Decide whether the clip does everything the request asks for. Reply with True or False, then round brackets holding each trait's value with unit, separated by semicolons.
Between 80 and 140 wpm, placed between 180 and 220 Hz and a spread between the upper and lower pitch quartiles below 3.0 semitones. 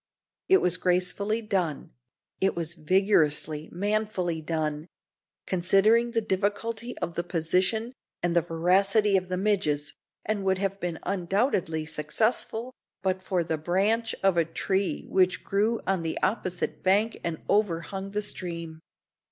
False (135 wpm; 190 Hz; 3.7 semitones)